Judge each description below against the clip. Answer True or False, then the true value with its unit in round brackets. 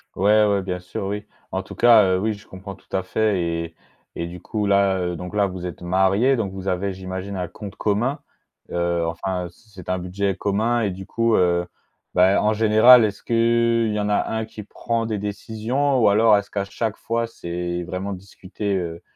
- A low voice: True (100 Hz)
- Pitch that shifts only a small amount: False (3.0 semitones)